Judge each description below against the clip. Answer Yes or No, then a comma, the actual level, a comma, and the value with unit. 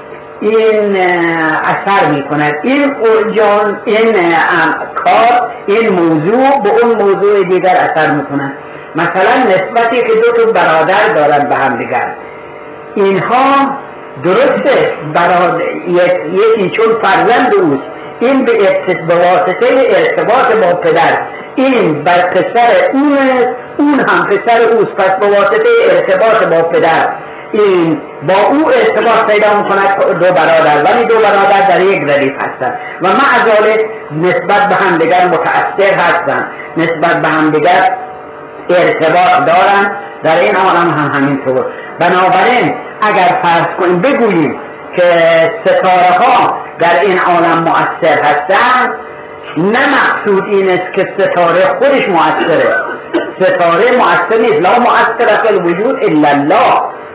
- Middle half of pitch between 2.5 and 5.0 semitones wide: No, wide, 5.5 semitones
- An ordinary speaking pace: Yes, average, 120 wpm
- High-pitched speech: Yes, high, 195 Hz